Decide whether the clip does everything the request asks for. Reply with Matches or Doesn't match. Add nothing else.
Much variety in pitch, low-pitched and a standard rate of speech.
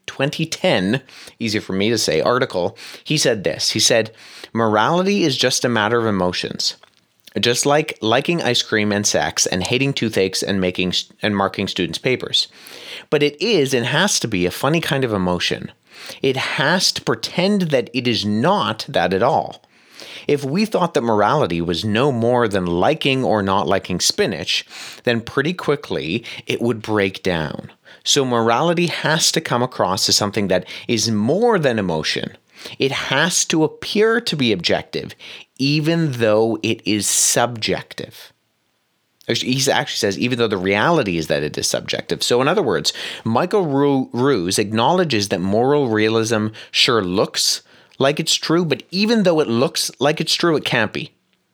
Matches